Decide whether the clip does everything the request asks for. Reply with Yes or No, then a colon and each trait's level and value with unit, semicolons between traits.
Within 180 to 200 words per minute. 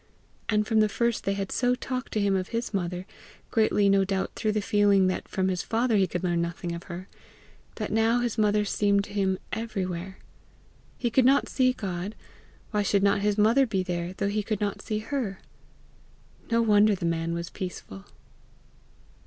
Yes: average, 190 wpm